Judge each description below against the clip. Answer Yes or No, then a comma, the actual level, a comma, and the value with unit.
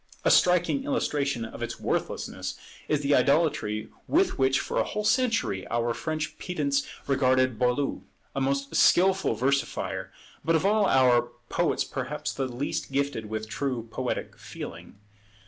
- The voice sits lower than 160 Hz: Yes, medium, 140 Hz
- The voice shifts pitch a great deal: No, average, 4.9 semitones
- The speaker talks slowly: No, average, 145 wpm